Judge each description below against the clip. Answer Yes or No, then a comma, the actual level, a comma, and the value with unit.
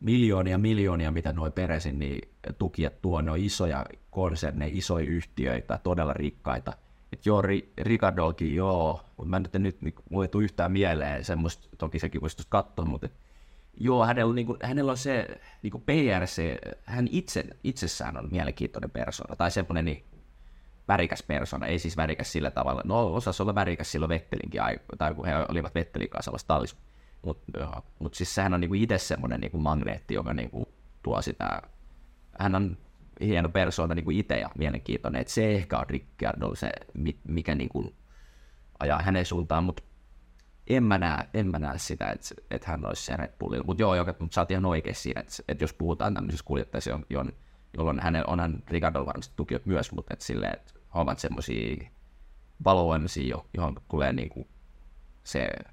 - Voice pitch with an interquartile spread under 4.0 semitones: No, average, 5.3 semitones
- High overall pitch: No, very low, 80 Hz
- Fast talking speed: Yes, fast, 175 wpm